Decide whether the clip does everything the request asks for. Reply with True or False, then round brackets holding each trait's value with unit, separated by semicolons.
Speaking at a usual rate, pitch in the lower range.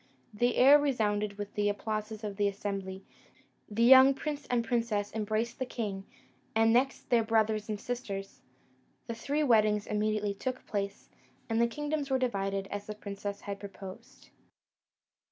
False (155 wpm; 215 Hz)